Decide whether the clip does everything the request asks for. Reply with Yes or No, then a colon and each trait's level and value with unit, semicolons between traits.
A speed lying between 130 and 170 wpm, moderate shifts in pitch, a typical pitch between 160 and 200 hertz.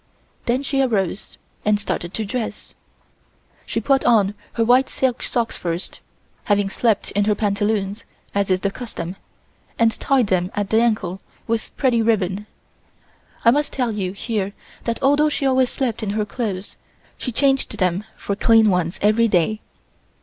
No: average, 160 wpm; average, 3.5 semitones; high, 215 Hz